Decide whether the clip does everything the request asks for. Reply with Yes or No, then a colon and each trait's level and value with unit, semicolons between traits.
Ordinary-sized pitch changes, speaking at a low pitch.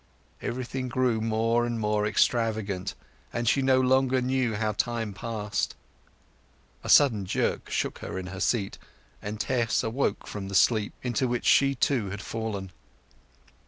Yes: average, 3.2 semitones; low, 115 Hz